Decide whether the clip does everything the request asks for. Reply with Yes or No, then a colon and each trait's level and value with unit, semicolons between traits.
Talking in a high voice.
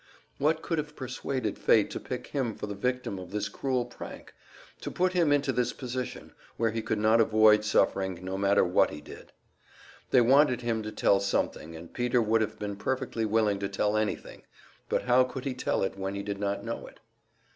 No: low, 110 Hz